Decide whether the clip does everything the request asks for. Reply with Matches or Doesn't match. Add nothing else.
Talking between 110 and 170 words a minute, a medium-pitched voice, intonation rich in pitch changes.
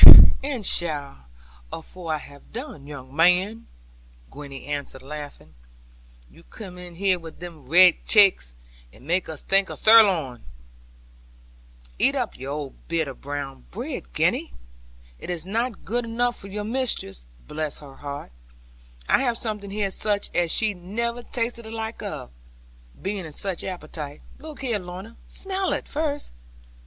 Matches